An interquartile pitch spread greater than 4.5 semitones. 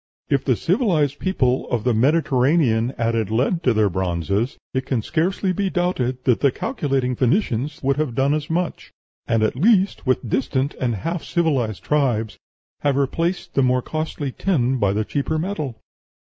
Yes: average, 5.0 semitones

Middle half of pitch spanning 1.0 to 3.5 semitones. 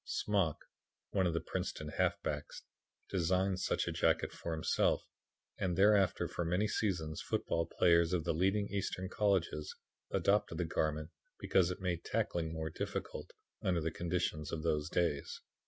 Yes: average, 2.8 semitones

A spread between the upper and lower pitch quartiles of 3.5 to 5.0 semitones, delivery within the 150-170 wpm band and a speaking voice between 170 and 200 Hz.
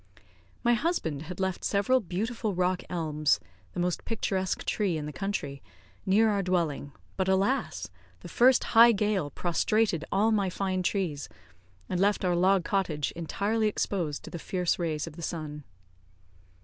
Yes: average, 3.8 semitones; average, 155 wpm; medium, 185 Hz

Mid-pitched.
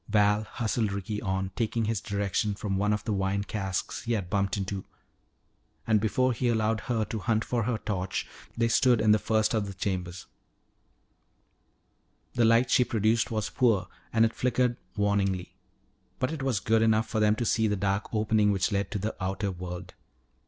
No: low, 105 Hz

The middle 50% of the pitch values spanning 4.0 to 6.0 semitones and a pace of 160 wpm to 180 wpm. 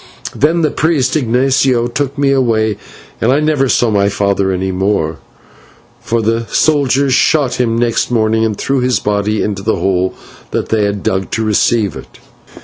Yes: average, 4.7 semitones; average, 170 wpm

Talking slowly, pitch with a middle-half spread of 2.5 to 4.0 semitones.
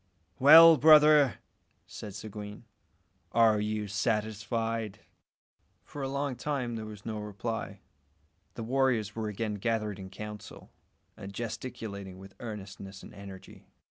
Yes: slow, 120 wpm; average, 2.8 semitones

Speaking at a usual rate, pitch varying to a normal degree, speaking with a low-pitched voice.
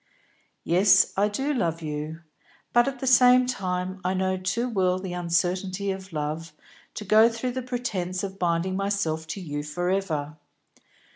No: average, 160 wpm; average, 3.7 semitones; medium, 185 Hz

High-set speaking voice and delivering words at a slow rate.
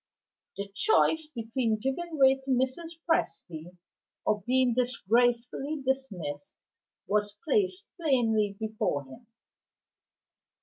Yes: high, 245 Hz; slow, 95 wpm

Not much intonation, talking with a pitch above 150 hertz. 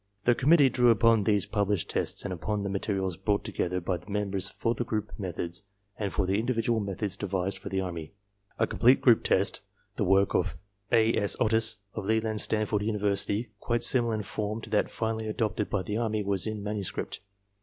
No: narrow, 2.3 semitones; low, 105 Hz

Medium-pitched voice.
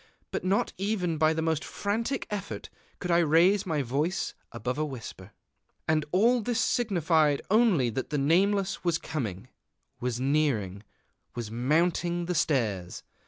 Yes: medium, 160 Hz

